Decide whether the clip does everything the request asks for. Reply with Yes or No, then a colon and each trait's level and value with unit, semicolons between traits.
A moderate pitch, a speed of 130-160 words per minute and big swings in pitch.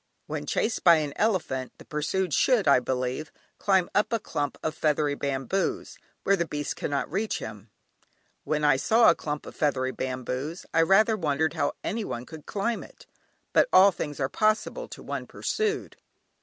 No: medium, 155 Hz; average, 170 wpm; wide, 5.9 semitones